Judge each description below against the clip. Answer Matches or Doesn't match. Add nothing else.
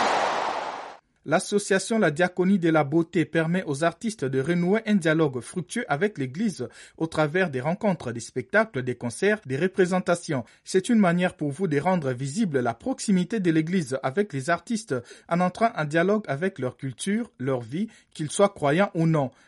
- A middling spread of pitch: Doesn't match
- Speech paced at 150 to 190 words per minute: Matches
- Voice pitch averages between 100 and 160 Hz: Doesn't match